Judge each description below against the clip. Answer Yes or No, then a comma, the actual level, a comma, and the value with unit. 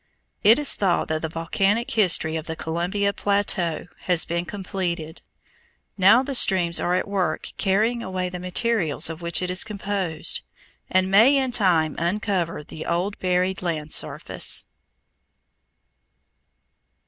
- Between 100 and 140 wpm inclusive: Yes, slow, 135 wpm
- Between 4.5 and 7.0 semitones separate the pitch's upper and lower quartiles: No, average, 3.2 semitones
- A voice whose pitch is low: No, medium, 185 Hz